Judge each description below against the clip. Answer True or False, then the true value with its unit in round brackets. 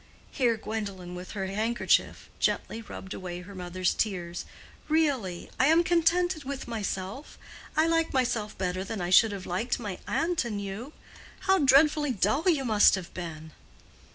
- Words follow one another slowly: False (155 wpm)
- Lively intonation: True (7.1 semitones)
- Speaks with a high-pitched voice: True (220 Hz)